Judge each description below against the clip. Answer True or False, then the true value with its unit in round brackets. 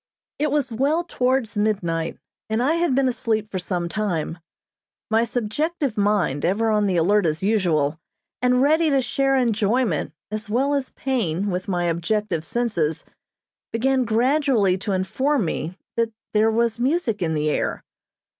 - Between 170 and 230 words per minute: False (155 wpm)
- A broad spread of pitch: True (5.8 semitones)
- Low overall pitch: False (220 Hz)